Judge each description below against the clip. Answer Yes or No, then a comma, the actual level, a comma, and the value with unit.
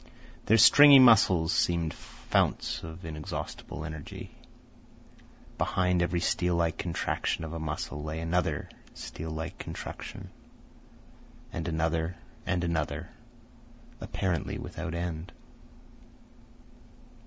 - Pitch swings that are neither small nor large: No, narrow, 1.8 semitones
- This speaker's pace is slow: Yes, slow, 95 wpm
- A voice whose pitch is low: Yes, very low, 85 Hz